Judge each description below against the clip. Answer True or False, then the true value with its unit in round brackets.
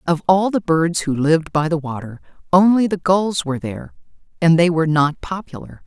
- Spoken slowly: False (195 wpm)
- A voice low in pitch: False (165 Hz)